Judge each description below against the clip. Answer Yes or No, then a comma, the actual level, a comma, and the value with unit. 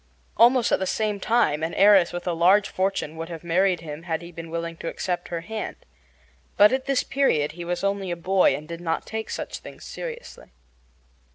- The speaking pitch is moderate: Yes, medium, 175 Hz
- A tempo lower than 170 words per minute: No, fast, 205 wpm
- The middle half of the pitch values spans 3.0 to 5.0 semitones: Yes, average, 3.8 semitones